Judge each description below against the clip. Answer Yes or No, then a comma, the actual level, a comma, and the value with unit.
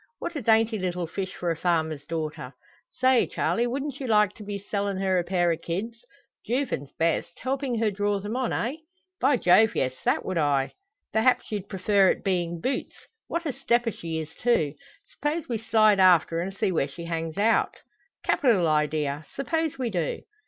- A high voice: Yes, high, 200 Hz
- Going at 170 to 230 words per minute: Yes, average, 185 wpm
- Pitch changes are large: Yes, wide, 5.9 semitones